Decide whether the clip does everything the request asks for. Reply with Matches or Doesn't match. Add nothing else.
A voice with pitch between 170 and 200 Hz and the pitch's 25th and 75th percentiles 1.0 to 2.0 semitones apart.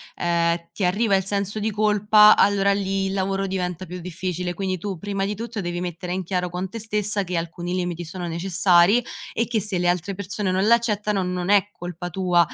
Doesn't match